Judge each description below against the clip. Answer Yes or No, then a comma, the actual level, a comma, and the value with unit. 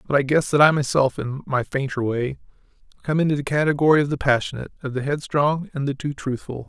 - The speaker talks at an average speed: No, fast, 215 wpm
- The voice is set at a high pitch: No, medium, 140 Hz